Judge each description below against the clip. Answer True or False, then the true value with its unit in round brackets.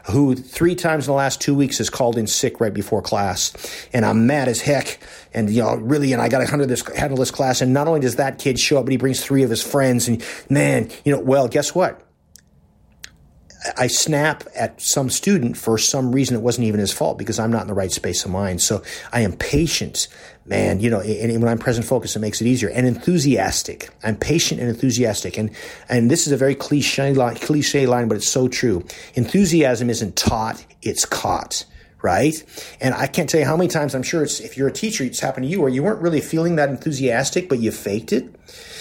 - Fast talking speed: True (230 wpm)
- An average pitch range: True (3.6 semitones)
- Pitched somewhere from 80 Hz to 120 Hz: False (130 Hz)